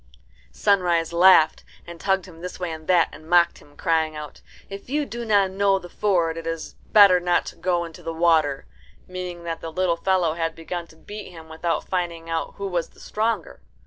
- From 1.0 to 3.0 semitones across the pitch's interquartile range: Yes, narrow, 2.4 semitones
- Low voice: No, medium, 175 Hz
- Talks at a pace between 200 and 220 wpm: Yes, fast, 205 wpm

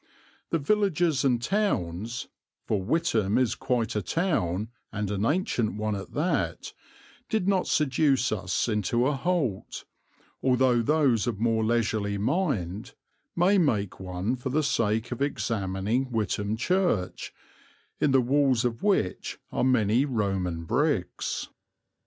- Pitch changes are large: Yes, wide, 5.7 semitones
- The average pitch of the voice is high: No, low, 120 Hz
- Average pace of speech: No, slow, 130 wpm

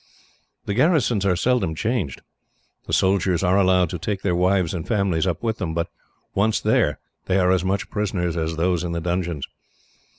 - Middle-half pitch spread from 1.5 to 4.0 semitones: Yes, narrow, 2.5 semitones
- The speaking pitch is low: Yes, very low, 95 Hz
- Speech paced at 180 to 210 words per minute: Yes, average, 185 wpm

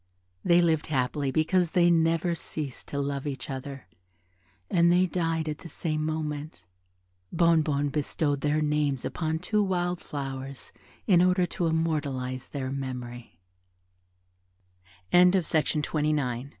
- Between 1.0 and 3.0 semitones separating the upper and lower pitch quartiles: No, average, 3.4 semitones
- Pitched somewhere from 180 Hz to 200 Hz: No, medium, 155 Hz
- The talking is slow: Yes, slow, 115 wpm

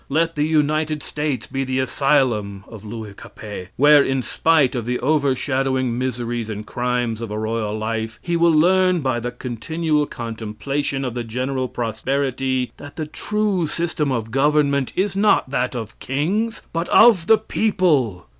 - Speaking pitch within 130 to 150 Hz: Yes, low, 135 Hz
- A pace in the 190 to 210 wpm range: No, average, 160 wpm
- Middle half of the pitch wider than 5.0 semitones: No, average, 4.7 semitones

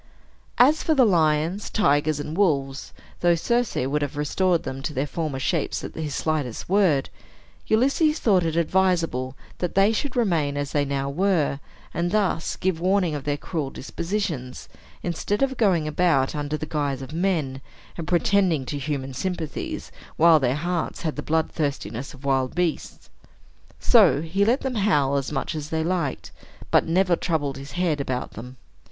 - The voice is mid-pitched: Yes, medium, 160 Hz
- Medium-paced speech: Yes, average, 170 wpm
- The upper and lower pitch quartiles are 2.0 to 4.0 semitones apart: No, average, 4.6 semitones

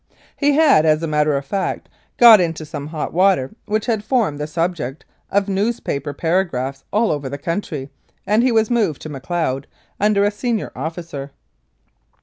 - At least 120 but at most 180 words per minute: Yes, average, 170 wpm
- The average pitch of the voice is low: No, medium, 170 Hz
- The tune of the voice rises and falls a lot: Yes, wide, 6.3 semitones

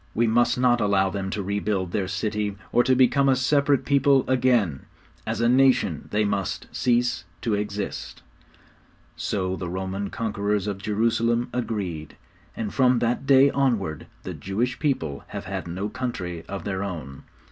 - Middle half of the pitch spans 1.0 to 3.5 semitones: No, average, 4.3 semitones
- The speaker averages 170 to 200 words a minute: No, average, 160 wpm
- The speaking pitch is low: Yes, low, 105 Hz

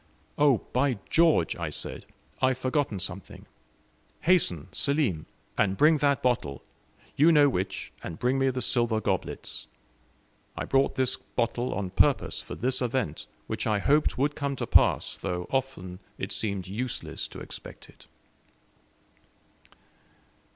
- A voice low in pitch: Yes, low, 125 Hz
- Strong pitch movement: Yes, wide, 6.1 semitones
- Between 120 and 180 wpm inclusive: Yes, average, 140 wpm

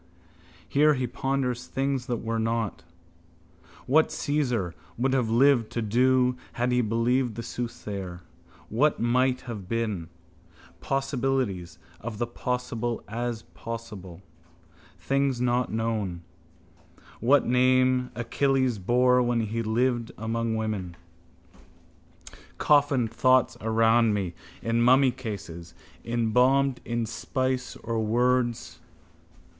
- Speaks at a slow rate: Yes, slow, 105 wpm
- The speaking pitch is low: Yes, low, 120 Hz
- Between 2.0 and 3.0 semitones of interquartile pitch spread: Yes, narrow, 2.4 semitones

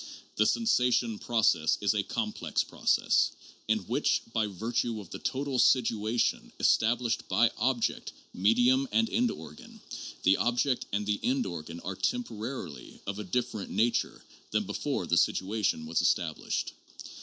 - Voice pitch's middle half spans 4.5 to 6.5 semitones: No, average, 3.6 semitones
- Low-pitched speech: Yes, low, 110 Hz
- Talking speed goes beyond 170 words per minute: No, average, 145 wpm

